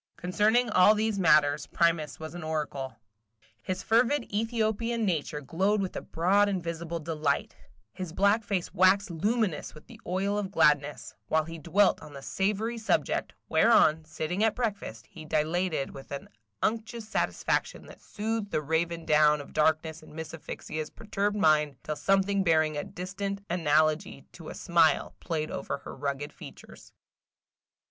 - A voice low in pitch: No, medium, 170 Hz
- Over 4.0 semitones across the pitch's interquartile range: Yes, average, 4.8 semitones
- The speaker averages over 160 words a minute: No, average, 155 wpm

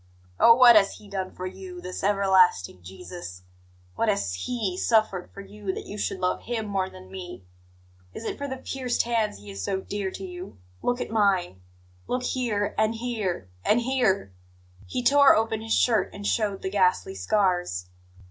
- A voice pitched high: Yes, high, 195 Hz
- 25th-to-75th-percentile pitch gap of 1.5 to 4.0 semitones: Yes, average, 3.7 semitones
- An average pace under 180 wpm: No, average, 185 wpm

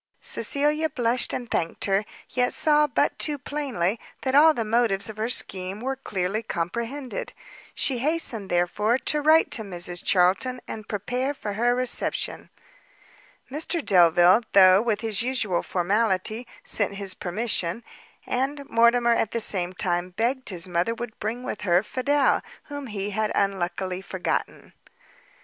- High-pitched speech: Yes, high, 220 Hz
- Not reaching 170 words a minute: Yes, average, 145 wpm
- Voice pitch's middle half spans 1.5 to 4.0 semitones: No, average, 5.1 semitones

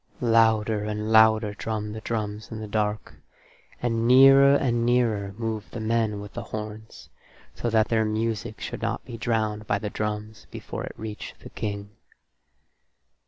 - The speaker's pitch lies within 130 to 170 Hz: No, low, 110 Hz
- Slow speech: No, average, 160 wpm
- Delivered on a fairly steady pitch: Yes, narrow, 1.3 semitones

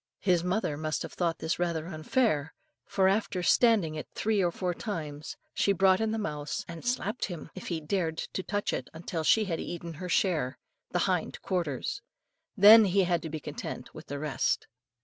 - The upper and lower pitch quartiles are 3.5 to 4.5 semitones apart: Yes, average, 4.1 semitones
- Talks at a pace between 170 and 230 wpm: Yes, average, 190 wpm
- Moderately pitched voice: Yes, medium, 175 Hz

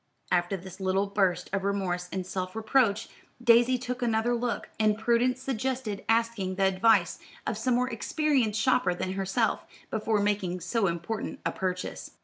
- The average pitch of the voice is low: No, high, 215 Hz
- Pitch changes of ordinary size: Yes, average, 4.0 semitones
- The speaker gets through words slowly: No, average, 155 wpm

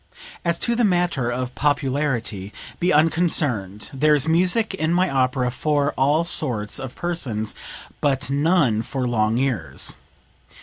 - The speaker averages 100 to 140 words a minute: Yes, slow, 135 wpm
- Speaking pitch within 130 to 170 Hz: Yes, medium, 140 Hz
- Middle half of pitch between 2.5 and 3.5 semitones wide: No, average, 5.2 semitones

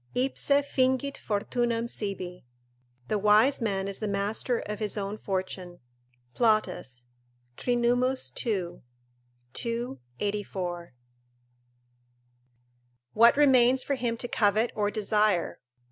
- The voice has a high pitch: Yes, high, 215 Hz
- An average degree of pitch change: Yes, average, 3.5 semitones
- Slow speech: Yes, slow, 100 wpm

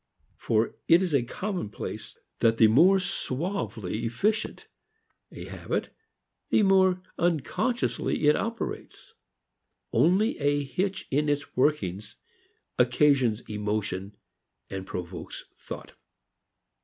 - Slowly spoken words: Yes, slow, 100 wpm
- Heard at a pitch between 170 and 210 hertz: No, medium, 145 Hz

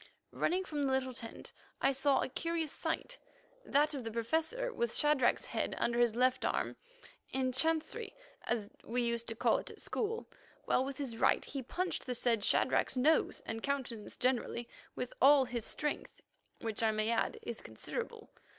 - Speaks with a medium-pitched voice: No, very high, 255 Hz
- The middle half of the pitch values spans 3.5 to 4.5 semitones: Yes, average, 4.1 semitones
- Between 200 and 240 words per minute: No, average, 175 wpm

